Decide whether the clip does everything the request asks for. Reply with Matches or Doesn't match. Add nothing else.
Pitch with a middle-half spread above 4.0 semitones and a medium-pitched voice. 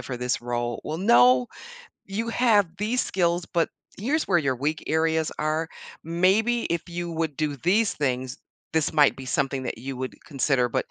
Matches